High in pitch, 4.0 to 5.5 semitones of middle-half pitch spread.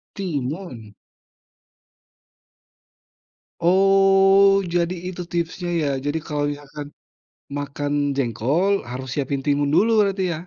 No: medium, 165 Hz; average, 5.2 semitones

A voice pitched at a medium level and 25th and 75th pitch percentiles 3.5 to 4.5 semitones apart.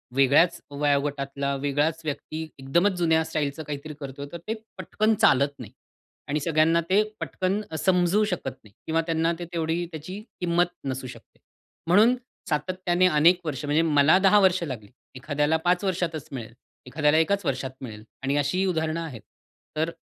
Yes: medium, 160 Hz; average, 3.8 semitones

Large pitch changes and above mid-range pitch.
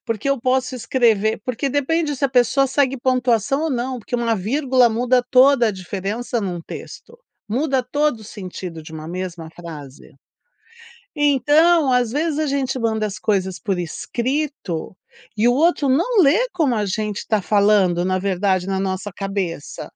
Yes: wide, 5.8 semitones; high, 235 Hz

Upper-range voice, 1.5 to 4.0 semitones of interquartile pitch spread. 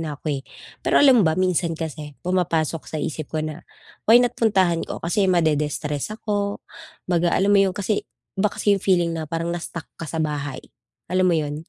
No: medium, 170 Hz; average, 3.7 semitones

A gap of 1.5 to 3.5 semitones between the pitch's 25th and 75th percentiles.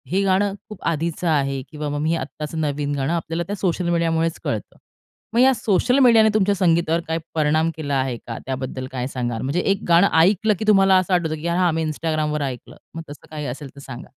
No: average, 4.1 semitones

